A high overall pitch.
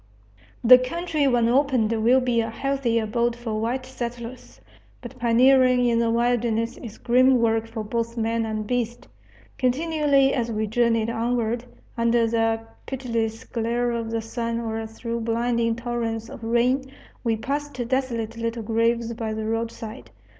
Yes: high, 235 Hz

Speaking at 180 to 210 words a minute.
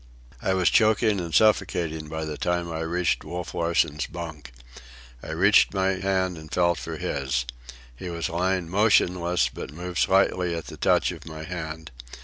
No: average, 165 wpm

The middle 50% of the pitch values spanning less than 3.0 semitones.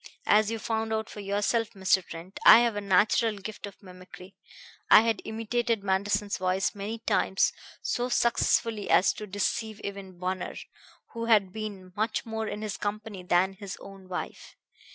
Yes: narrow, 2.6 semitones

